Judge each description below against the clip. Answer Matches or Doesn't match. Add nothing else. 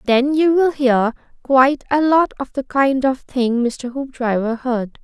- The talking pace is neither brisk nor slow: Matches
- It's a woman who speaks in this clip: Matches